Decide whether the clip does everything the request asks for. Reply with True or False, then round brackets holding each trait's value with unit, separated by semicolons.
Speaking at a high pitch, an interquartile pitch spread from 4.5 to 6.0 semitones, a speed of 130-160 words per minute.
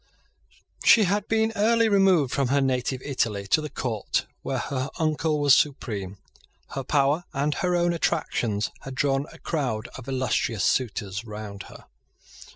False (135 Hz; 5.4 semitones; 155 wpm)